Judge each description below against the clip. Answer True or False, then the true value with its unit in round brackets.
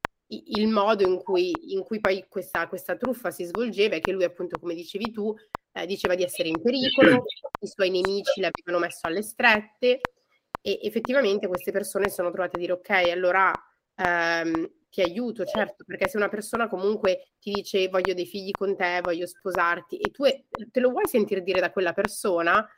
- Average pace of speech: False (185 wpm)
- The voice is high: True (195 Hz)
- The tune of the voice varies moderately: True (3.1 semitones)